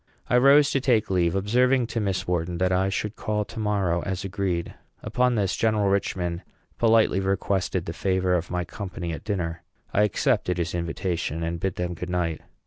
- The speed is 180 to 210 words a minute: Yes, average, 185 wpm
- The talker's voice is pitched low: Yes, very low, 95 Hz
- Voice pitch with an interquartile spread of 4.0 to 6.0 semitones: No, average, 3.3 semitones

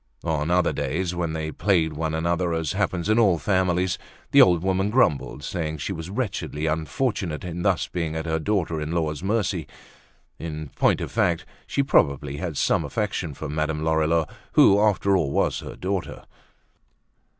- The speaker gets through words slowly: No, average, 170 wpm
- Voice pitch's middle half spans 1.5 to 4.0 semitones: Yes, average, 3.3 semitones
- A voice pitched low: Yes, very low, 85 Hz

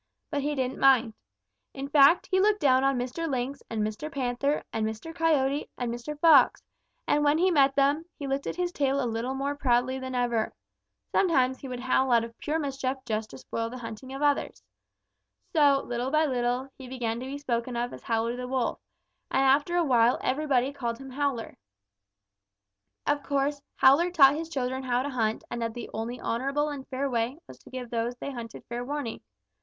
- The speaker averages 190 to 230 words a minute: Yes, average, 200 wpm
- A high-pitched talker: Yes, very high, 265 Hz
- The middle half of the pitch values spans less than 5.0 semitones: Yes, average, 2.9 semitones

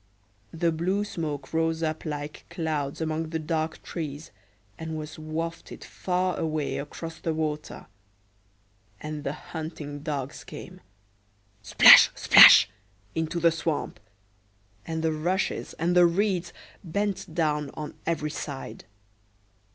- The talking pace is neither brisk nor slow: No, slow, 115 wpm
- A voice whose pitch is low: No, medium, 155 Hz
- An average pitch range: No, narrow, 2.2 semitones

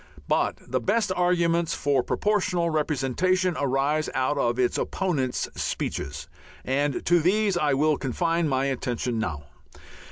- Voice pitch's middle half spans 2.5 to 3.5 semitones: No, average, 5.0 semitones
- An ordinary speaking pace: No, slow, 130 wpm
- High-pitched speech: No, medium, 150 Hz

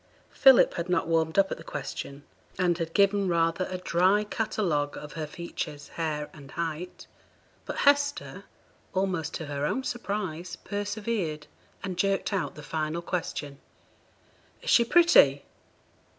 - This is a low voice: No, medium, 175 Hz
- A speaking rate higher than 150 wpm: No, average, 140 wpm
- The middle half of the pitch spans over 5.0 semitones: No, average, 4.6 semitones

